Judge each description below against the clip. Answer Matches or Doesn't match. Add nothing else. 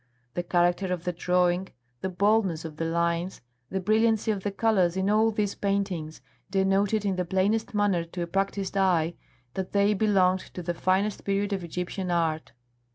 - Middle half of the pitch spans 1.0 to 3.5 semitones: Matches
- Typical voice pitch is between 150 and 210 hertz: Matches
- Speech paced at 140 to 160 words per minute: Doesn't match